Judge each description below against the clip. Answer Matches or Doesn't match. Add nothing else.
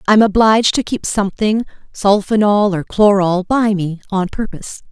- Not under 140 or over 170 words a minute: Matches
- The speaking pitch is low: Doesn't match